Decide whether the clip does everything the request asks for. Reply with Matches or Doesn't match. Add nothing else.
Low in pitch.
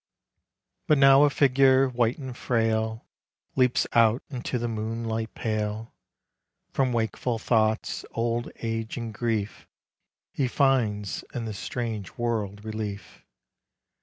Matches